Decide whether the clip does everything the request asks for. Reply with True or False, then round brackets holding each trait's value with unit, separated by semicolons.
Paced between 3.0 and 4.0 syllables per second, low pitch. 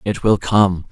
True (3.9 syllables/s; 100 Hz)